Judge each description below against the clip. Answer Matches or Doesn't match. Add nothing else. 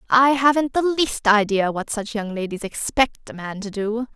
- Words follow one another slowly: Doesn't match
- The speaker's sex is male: Doesn't match